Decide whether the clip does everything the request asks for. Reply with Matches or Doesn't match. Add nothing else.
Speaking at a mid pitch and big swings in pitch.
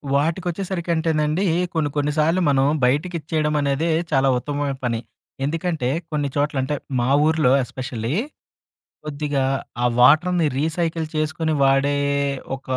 Doesn't match